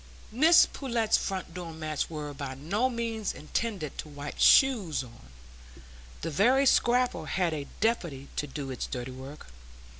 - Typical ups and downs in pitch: No, wide, 8.2 semitones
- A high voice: No, medium, 165 Hz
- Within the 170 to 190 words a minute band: No, average, 150 wpm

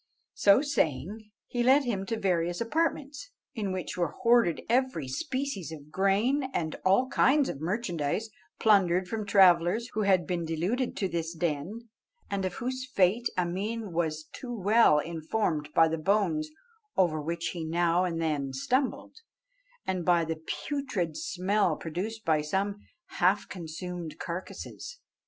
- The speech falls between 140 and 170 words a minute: Yes, average, 145 wpm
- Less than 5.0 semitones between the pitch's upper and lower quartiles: No, wide, 5.5 semitones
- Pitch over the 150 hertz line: Yes, medium, 185 Hz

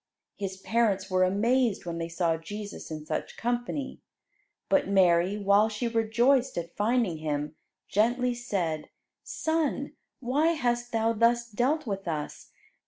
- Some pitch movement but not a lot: Yes, average, 4.8 semitones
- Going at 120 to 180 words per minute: Yes, slow, 135 wpm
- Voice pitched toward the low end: No, high, 220 Hz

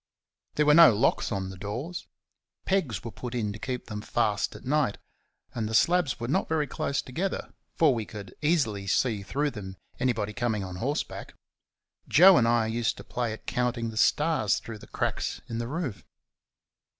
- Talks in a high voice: No, low, 120 Hz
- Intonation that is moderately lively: No, wide, 5.7 semitones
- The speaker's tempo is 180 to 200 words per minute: Yes, average, 185 wpm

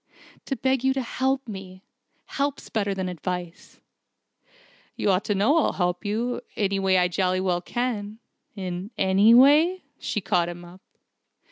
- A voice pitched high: Yes, high, 200 Hz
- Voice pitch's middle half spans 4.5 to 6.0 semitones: Yes, average, 5.2 semitones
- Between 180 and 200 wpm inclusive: No, average, 165 wpm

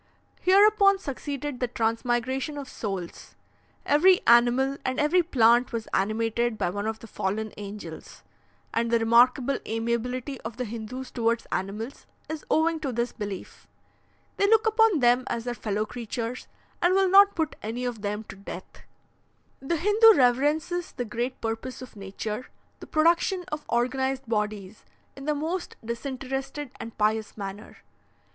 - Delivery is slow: No, average, 150 wpm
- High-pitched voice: Yes, high, 245 Hz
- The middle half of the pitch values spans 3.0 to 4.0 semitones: No, average, 4.8 semitones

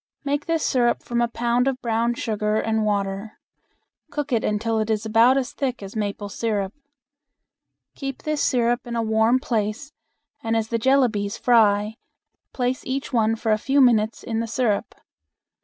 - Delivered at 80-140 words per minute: No, average, 170 wpm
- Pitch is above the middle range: Yes, high, 230 Hz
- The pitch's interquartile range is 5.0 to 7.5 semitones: No, average, 2.8 semitones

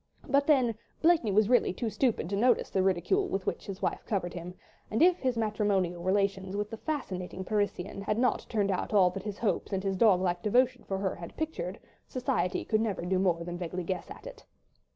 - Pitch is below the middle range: No, high, 200 Hz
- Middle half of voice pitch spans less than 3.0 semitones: No, average, 4.2 semitones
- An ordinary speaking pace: No, fast, 215 wpm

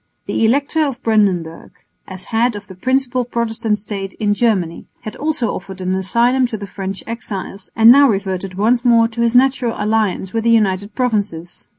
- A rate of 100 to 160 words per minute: No, average, 180 wpm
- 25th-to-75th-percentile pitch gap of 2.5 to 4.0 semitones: Yes, average, 3.6 semitones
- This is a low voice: No, high, 220 Hz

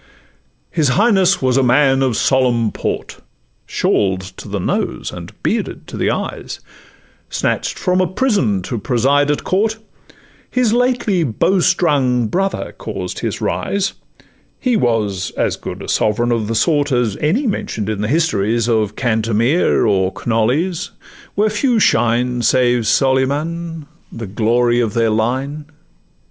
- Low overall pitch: Yes, low, 130 Hz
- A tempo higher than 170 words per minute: No, average, 140 wpm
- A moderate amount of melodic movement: No, wide, 7.1 semitones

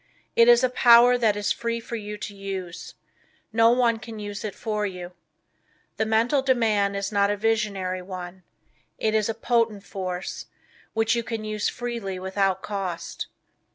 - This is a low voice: No, high, 215 Hz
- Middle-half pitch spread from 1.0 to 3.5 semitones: Yes, average, 2.8 semitones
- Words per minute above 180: No, average, 165 wpm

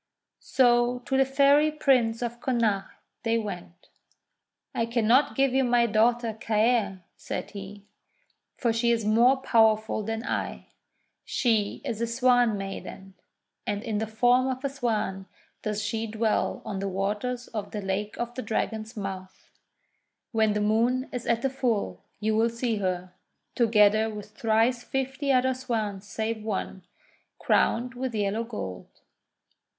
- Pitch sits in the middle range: No, high, 225 Hz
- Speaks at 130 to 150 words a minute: Yes, average, 145 wpm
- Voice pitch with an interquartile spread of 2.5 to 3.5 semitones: Yes, average, 2.8 semitones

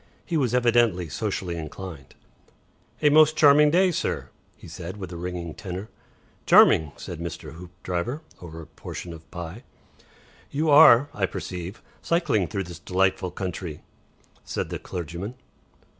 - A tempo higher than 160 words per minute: No, average, 140 wpm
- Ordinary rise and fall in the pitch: No, wide, 6.1 semitones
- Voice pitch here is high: No, very low, 90 Hz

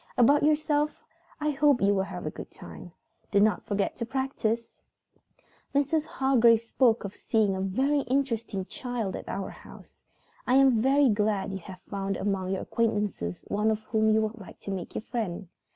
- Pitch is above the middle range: Yes, high, 220 Hz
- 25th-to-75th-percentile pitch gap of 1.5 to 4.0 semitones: No, average, 5.0 semitones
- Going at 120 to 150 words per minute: No, average, 175 wpm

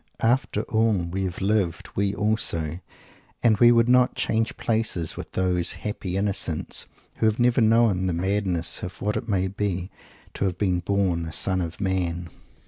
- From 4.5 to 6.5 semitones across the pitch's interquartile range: No, average, 3.5 semitones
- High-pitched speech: No, very low, 95 Hz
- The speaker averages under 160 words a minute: No, average, 170 wpm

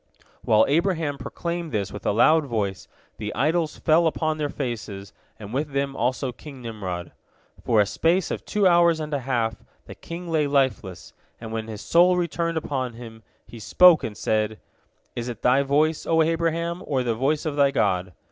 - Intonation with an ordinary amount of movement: No, wide, 6.4 semitones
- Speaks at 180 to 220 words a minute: Yes, average, 185 wpm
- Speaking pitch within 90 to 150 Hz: Yes, medium, 140 Hz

